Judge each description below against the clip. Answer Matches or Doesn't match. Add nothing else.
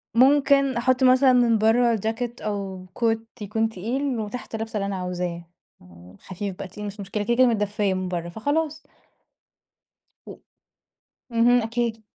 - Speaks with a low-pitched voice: Doesn't match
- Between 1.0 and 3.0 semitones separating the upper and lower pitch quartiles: Doesn't match